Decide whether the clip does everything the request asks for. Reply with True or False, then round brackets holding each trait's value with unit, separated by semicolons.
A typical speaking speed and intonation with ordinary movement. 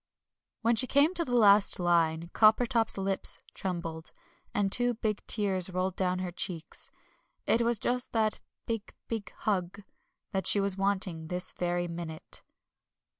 True (145 wpm; 4.1 semitones)